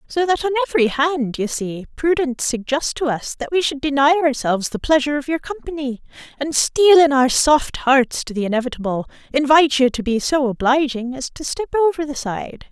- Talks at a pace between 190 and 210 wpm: Yes, average, 195 wpm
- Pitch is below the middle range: No, very high, 280 Hz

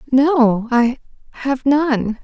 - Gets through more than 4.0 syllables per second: No, 2.7 syllables/s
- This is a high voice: Yes, very high, 260 Hz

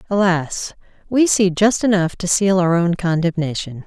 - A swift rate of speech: No, average, 155 wpm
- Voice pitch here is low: No, medium, 180 Hz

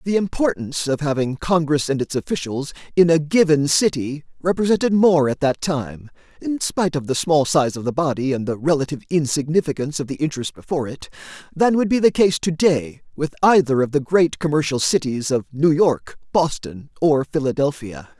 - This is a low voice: No, medium, 150 Hz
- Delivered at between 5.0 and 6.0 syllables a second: Yes, 5.4 syllables/s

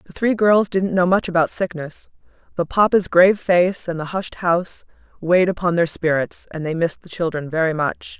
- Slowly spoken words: No, average, 200 wpm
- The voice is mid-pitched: Yes, medium, 175 Hz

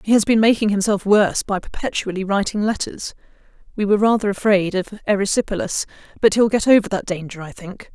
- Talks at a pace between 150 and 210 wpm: Yes, average, 180 wpm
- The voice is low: No, high, 200 Hz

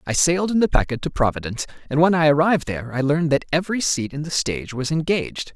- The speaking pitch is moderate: Yes, medium, 150 Hz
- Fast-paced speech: Yes, fast, 235 wpm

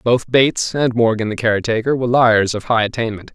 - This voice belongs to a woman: No, male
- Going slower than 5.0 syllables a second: No, 5.9 syllables/s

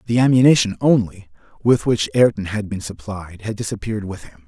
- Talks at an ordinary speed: Yes, average, 175 wpm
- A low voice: Yes, low, 105 Hz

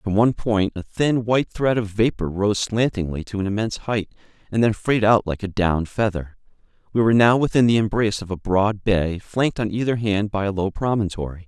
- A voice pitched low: Yes, low, 105 Hz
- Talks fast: Yes, fast, 215 wpm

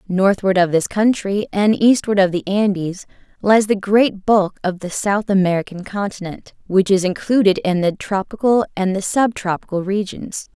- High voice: Yes, high, 195 Hz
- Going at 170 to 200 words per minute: No, average, 160 wpm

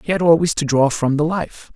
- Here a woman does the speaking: No, male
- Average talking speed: No, fast, 275 wpm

